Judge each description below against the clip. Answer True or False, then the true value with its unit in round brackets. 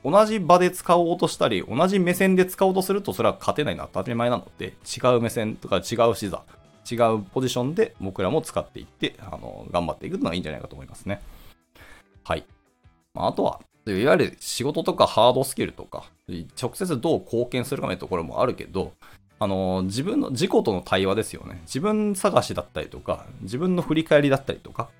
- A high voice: False (115 Hz)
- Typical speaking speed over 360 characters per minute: True (405 characters per minute)